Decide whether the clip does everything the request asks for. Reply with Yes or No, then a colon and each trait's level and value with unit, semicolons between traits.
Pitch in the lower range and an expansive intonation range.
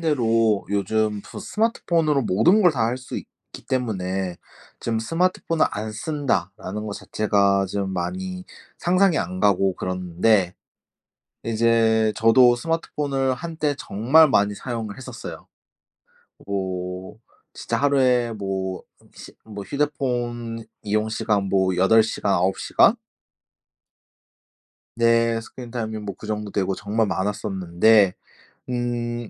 No: low, 110 Hz; average, 4.5 semitones